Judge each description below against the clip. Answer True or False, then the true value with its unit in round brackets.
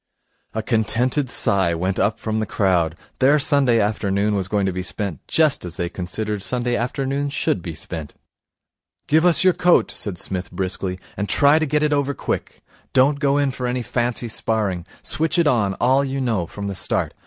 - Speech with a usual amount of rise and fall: False (6.2 semitones)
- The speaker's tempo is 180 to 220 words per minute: True (190 wpm)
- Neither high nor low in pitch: False (110 Hz)